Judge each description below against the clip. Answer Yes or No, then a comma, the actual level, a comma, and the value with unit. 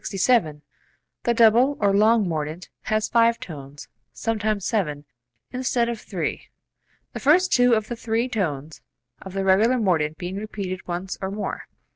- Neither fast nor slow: Yes, average, 155 wpm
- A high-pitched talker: Yes, high, 210 Hz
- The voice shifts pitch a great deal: No, average, 4.7 semitones